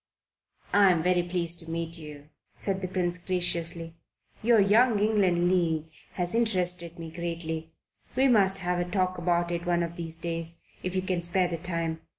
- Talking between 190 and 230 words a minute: No, average, 170 wpm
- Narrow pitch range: Yes, narrow, 1.8 semitones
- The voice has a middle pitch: Yes, medium, 175 Hz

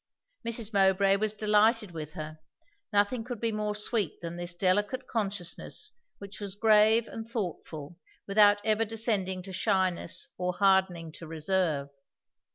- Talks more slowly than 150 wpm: Yes, average, 140 wpm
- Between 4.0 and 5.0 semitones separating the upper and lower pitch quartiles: No, average, 3.3 semitones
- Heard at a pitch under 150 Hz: No, high, 200 Hz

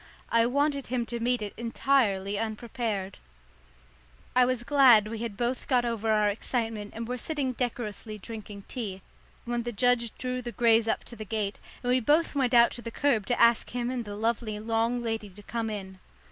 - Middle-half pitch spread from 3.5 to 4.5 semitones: No, narrow, 2.5 semitones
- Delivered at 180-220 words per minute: Yes, average, 195 wpm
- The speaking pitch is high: Yes, high, 235 Hz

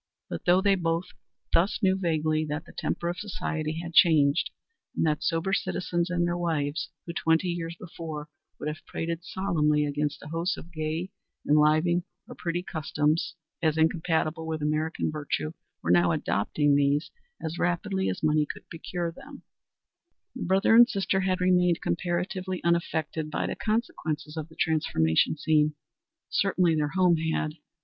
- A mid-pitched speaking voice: Yes, medium, 165 Hz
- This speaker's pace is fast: No, average, 155 wpm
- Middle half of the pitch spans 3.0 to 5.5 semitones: No, narrow, 2.5 semitones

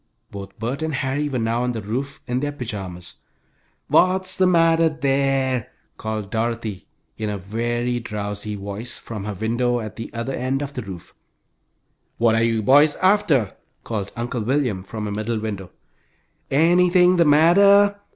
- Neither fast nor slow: Yes, average, 160 wpm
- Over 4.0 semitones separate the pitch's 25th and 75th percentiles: Yes, average, 5.2 semitones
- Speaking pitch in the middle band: No, low, 120 Hz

